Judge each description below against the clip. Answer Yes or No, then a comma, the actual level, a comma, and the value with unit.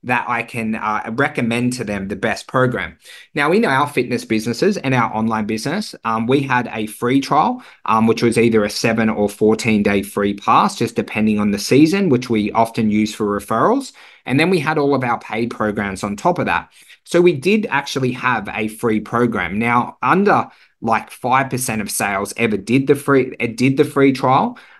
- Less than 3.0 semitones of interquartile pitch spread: No, average, 3.5 semitones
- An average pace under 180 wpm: No, average, 195 wpm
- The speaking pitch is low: Yes, low, 115 Hz